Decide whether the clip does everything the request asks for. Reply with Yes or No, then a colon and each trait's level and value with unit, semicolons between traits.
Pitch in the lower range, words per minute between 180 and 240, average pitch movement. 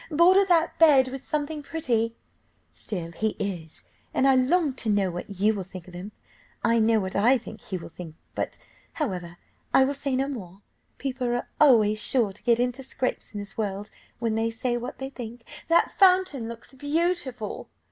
No: high, 240 Hz; average, 190 wpm; average, 5.0 semitones